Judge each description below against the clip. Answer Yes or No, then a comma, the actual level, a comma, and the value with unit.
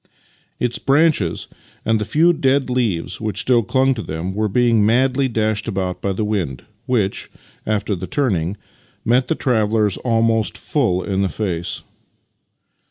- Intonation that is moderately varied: Yes, average, 4.5 semitones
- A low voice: Yes, low, 110 Hz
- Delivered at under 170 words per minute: Yes, average, 150 wpm